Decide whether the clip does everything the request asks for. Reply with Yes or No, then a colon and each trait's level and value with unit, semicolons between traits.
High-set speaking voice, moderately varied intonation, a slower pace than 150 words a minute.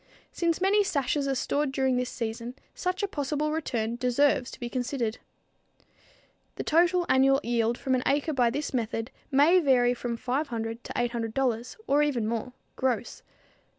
No: very high, 260 Hz; average, 3.6 semitones; average, 155 wpm